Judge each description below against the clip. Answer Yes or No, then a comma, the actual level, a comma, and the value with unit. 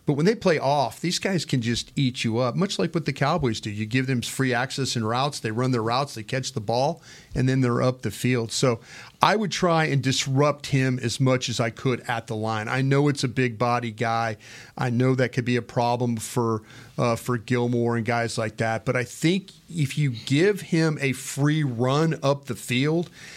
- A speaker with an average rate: No, fast, 230 wpm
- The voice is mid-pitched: No, low, 130 Hz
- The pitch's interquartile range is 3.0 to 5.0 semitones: Yes, average, 3.3 semitones